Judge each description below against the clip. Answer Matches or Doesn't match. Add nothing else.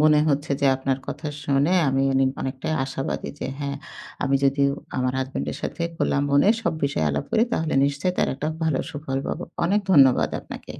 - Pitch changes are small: Matches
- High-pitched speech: Doesn't match